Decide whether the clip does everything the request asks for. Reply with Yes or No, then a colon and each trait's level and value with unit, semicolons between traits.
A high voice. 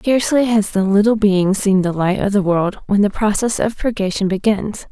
Yes: high, 205 Hz